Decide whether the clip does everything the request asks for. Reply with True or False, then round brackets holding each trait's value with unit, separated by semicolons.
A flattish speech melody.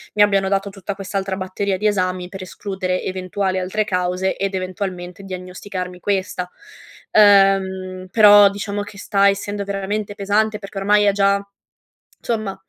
True (1.5 semitones)